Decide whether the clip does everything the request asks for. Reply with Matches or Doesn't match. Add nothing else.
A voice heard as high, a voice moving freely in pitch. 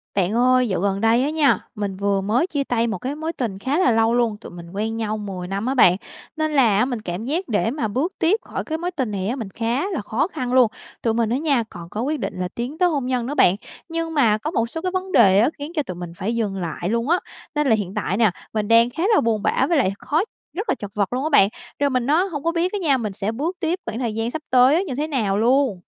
Matches